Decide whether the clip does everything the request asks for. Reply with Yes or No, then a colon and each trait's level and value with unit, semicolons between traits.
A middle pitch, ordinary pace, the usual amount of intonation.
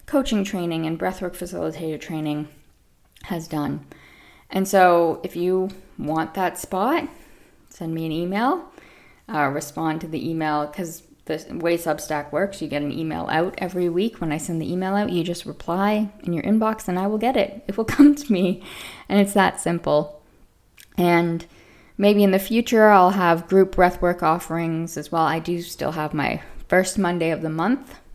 Yes: medium, 175 Hz; average, 180 wpm; average, 3.6 semitones